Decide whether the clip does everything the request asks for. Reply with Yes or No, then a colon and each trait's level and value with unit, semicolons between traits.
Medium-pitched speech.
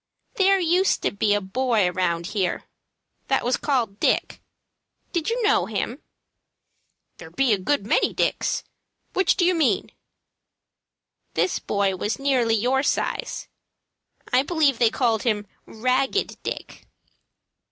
No: high, 245 Hz